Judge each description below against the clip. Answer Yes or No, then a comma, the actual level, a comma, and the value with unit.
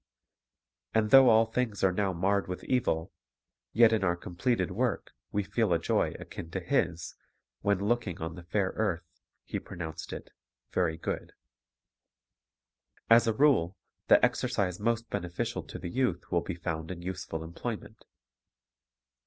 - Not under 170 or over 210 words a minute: No, average, 155 wpm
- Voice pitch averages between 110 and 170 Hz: No, very low, 95 Hz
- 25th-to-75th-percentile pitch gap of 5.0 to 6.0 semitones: No, average, 4.5 semitones